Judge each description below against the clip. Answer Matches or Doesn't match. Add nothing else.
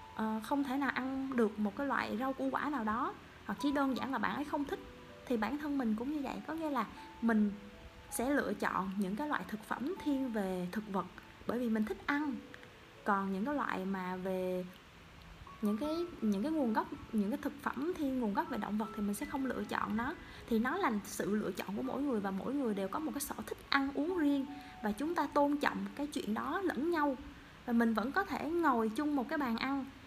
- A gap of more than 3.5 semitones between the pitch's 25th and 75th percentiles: Matches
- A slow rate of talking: Doesn't match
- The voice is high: Matches